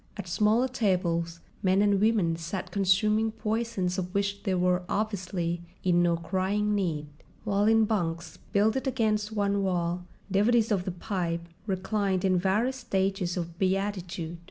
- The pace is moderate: Yes, average, 145 wpm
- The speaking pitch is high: Yes, high, 195 Hz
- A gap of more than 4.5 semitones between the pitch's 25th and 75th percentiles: No, average, 3.0 semitones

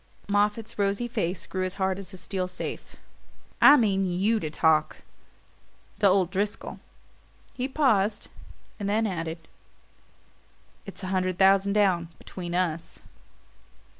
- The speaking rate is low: Yes, slow, 130 wpm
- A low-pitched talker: No, high, 195 Hz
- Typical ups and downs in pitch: No, narrow, 2.3 semitones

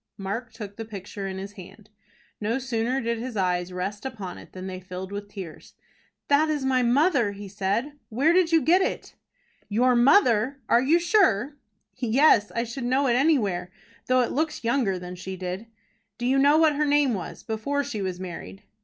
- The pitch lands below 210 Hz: No, high, 230 Hz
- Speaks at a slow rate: No, average, 190 wpm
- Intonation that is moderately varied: No, wide, 5.7 semitones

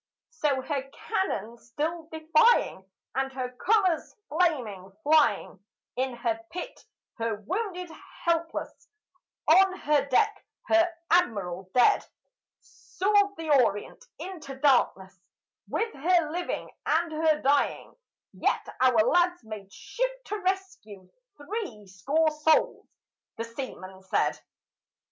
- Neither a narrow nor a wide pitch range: No, wide, 7.3 semitones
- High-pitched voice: Yes, very high, 300 Hz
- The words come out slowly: Yes, slow, 110 wpm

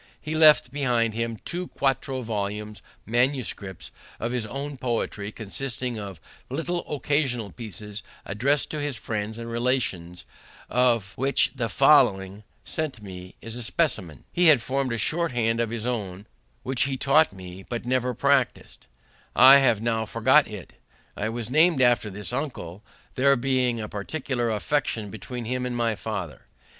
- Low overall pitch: Yes, low, 120 Hz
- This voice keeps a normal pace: Yes, average, 160 wpm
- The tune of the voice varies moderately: Yes, average, 4.2 semitones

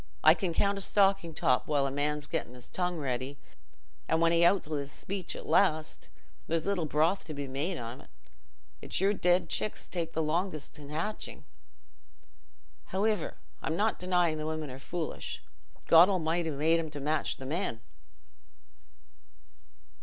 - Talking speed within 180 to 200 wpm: No, average, 155 wpm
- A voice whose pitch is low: No, medium, 160 Hz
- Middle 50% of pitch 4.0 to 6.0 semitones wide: No, average, 3.4 semitones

